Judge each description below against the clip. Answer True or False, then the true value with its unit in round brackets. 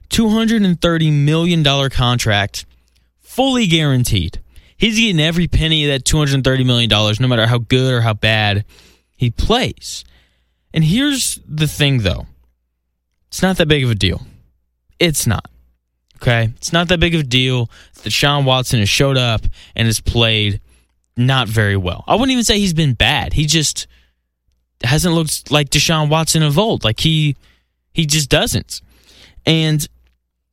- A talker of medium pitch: False (125 Hz)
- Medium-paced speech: True (170 wpm)